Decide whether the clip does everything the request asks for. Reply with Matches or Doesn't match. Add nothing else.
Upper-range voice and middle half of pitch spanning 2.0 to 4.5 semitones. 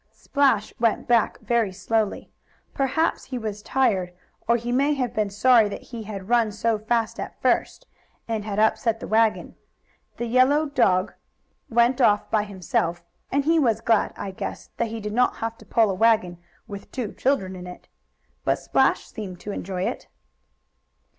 Matches